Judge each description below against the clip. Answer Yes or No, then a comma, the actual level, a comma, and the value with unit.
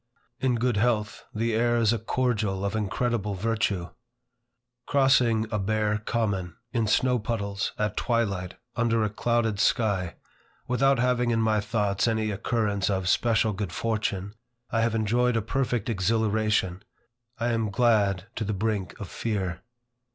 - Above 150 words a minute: No, average, 145 wpm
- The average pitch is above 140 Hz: No, low, 110 Hz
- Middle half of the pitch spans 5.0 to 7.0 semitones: No, narrow, 2.6 semitones